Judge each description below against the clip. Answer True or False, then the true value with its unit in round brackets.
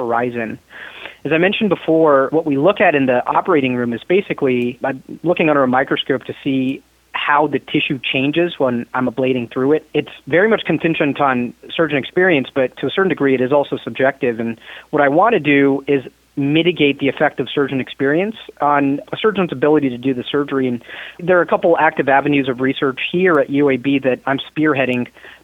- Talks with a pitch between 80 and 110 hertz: False (140 Hz)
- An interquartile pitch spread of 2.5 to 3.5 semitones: True (2.9 semitones)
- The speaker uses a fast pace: False (195 wpm)